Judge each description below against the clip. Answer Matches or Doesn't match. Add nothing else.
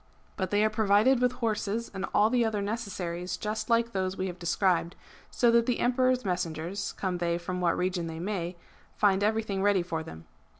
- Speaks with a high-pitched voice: Matches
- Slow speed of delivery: Doesn't match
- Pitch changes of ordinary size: Matches